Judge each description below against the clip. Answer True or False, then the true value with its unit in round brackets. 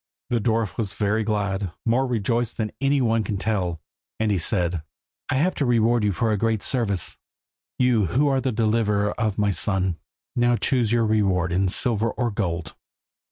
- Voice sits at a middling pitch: False (110 Hz)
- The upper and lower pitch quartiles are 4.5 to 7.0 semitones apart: False (3.2 semitones)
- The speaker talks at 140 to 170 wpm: False (180 wpm)